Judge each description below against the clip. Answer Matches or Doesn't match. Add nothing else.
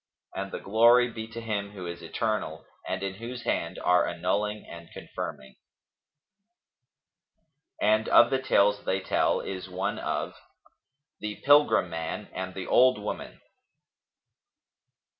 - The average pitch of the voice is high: Doesn't match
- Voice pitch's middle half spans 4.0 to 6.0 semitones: Doesn't match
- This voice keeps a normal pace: Doesn't match